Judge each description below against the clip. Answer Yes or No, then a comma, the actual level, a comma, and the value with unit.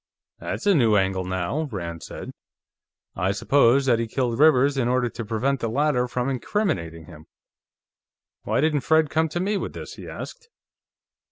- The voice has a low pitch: Yes, low, 125 Hz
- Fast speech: No, average, 170 wpm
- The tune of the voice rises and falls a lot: Yes, wide, 6.1 semitones